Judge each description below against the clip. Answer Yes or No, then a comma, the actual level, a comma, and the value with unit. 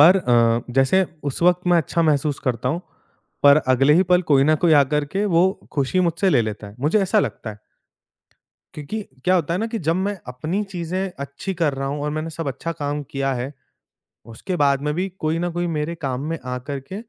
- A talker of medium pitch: Yes, medium, 155 Hz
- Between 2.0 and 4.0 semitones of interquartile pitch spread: No, average, 4.5 semitones